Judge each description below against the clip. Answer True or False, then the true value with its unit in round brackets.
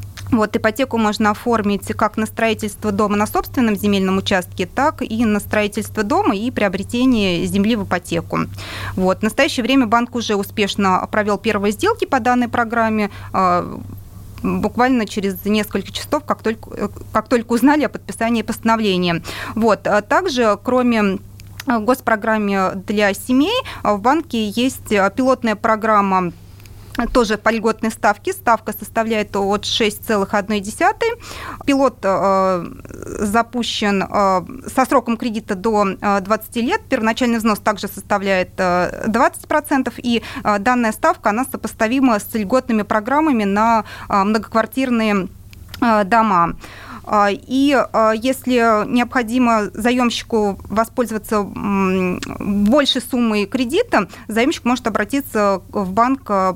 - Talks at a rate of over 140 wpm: False (120 wpm)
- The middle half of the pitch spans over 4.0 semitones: False (3.2 semitones)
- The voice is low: False (220 Hz)